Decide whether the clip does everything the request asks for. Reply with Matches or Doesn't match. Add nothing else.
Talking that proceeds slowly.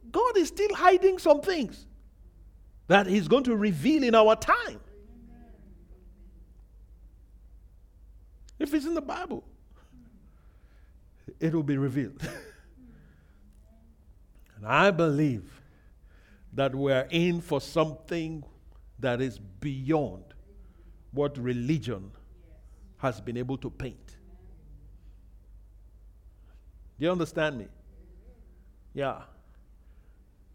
Matches